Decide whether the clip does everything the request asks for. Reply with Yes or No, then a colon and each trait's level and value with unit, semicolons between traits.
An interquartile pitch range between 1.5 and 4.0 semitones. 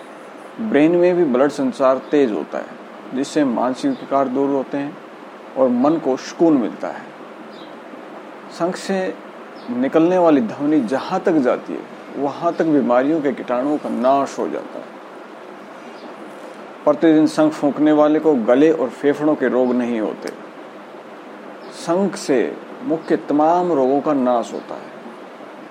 Yes: average, 3.7 semitones